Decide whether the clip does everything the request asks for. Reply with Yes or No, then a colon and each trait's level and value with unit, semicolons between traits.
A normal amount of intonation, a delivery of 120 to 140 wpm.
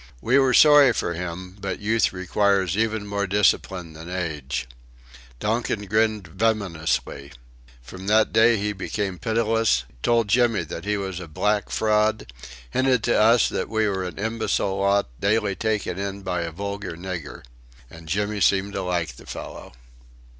No: average, 3.2 semitones; average, 155 wpm